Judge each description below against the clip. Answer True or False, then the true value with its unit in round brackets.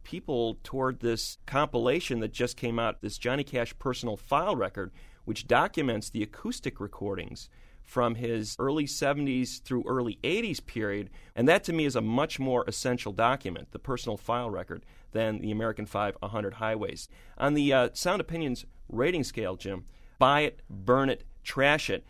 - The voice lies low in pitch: True (120 Hz)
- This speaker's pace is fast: False (165 wpm)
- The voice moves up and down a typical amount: True (3.7 semitones)